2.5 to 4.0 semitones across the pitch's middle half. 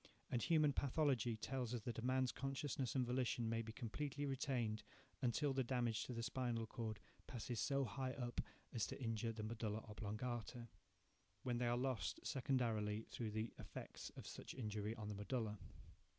Yes: average, 2.8 semitones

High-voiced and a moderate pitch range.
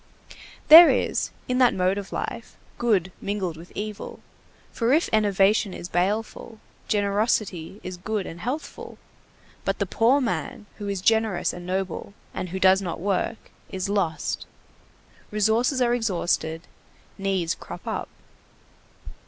Yes: high, 200 Hz; average, 3.4 semitones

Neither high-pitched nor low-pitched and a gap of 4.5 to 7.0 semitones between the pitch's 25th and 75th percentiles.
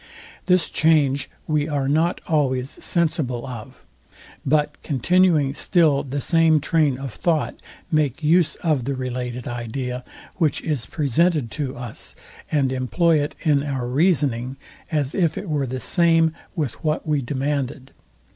No: medium, 145 Hz; average, 3.5 semitones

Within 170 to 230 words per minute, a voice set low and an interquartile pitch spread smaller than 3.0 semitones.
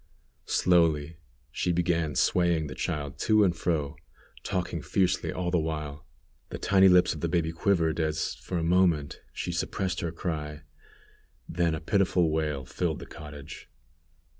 No: average, 150 wpm; very low, 80 Hz; narrow, 2.6 semitones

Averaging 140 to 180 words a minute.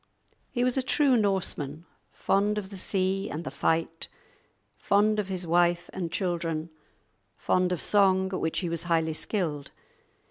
Yes: average, 155 wpm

